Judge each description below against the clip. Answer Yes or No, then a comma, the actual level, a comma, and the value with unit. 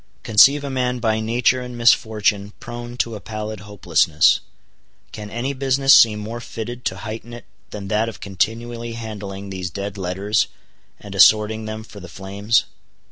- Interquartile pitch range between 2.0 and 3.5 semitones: Yes, average, 2.7 semitones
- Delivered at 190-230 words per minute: No, average, 160 wpm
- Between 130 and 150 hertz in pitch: No, low, 110 Hz